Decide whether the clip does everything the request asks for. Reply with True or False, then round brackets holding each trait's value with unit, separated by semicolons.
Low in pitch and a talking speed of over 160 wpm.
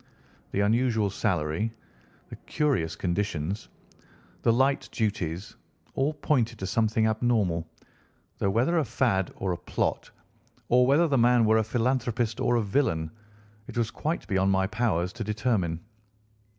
False (110 Hz; 140 wpm)